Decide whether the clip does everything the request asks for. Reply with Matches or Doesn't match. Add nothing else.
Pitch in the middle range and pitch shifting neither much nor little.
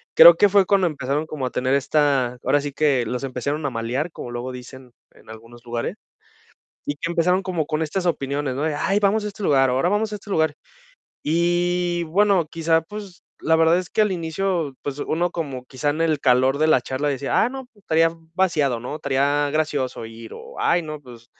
Matches